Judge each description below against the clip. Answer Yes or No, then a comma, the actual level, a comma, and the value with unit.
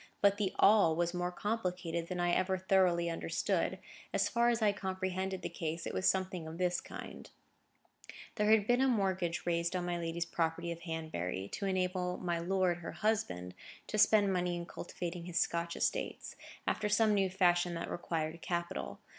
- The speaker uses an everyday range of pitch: No, narrow, 2.2 semitones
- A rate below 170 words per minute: No, average, 175 wpm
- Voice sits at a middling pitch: Yes, medium, 180 Hz